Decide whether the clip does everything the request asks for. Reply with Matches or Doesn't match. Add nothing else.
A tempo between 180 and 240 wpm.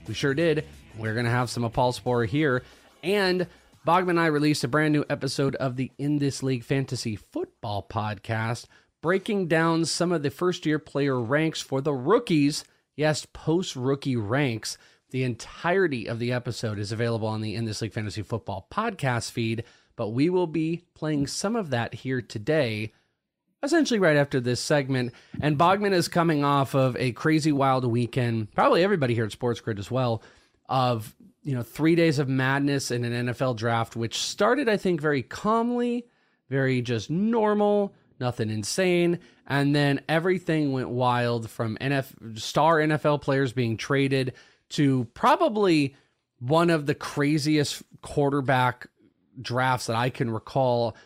Doesn't match